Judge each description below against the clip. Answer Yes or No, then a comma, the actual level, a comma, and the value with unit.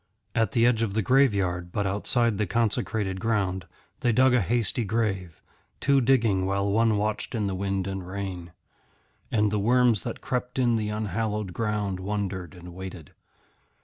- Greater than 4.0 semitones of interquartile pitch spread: No, average, 3.2 semitones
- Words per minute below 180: Yes, average, 165 wpm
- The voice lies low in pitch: Yes, low, 105 Hz